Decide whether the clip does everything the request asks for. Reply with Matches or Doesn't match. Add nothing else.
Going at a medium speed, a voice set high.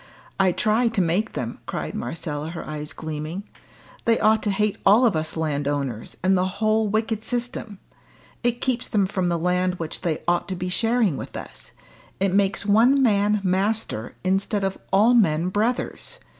Matches